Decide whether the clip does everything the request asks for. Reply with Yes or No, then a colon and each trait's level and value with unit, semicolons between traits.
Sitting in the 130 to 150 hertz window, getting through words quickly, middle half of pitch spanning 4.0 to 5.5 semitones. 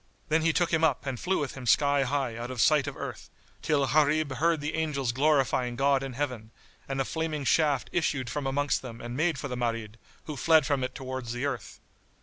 No: medium, 140 Hz; fast, 220 wpm; average, 3.1 semitones